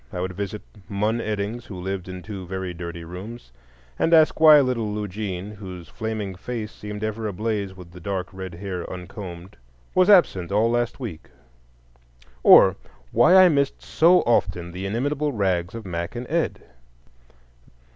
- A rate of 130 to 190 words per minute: Yes, average, 155 wpm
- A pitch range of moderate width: Yes, average, 4.3 semitones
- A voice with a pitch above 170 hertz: No, low, 105 Hz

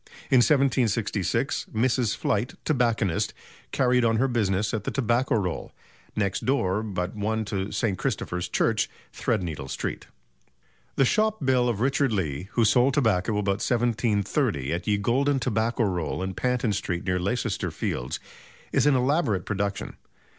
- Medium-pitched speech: No, low, 110 Hz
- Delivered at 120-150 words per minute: Yes, average, 145 wpm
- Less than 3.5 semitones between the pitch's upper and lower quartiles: No, average, 4.4 semitones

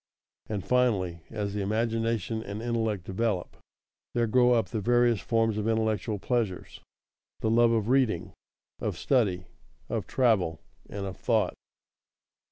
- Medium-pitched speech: No, low, 110 Hz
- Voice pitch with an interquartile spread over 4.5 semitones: No, narrow, 2.6 semitones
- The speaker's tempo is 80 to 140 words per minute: Yes, slow, 135 wpm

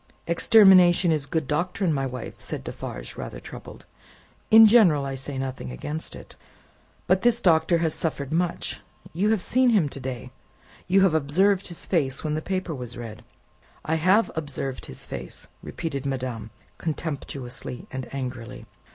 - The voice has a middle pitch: Yes, medium, 155 Hz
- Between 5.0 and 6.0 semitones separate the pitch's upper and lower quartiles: Yes, wide, 5.6 semitones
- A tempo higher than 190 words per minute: No, average, 155 wpm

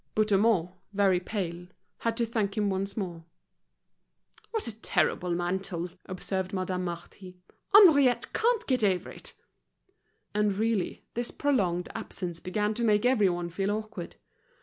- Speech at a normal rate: No, slow, 130 wpm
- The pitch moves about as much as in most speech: Yes, average, 3.7 semitones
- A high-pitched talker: Yes, high, 200 Hz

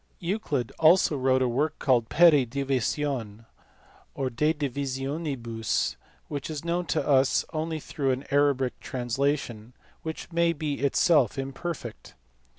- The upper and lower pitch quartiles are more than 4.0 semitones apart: No, average, 3.4 semitones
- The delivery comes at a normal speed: No, slow, 125 wpm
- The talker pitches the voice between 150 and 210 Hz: No, medium, 140 Hz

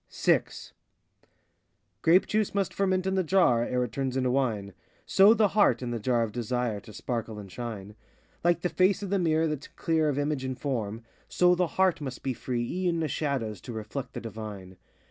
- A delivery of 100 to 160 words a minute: No, fast, 205 wpm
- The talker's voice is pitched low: Yes, low, 130 Hz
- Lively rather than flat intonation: Yes, wide, 7.4 semitones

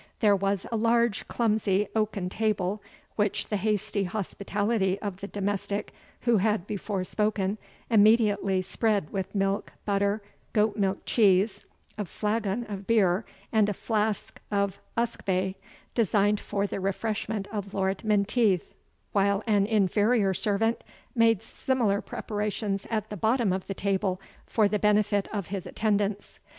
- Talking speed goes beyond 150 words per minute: No, average, 140 wpm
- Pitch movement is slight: Yes, narrow, 1.7 semitones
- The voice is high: Yes, high, 205 Hz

